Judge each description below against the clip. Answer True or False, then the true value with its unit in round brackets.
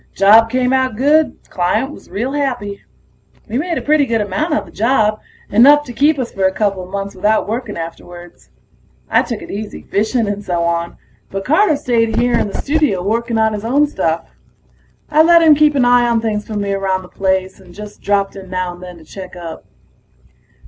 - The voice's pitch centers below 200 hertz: False (215 Hz)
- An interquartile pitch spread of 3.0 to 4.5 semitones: False (5.2 semitones)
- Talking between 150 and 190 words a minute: False (205 wpm)